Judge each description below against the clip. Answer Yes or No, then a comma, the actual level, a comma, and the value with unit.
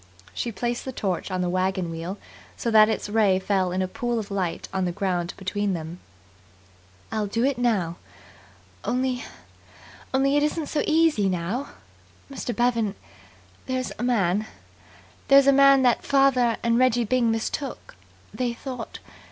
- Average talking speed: Yes, average, 155 wpm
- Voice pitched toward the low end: No, high, 225 Hz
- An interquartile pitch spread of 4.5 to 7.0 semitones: Yes, average, 5.2 semitones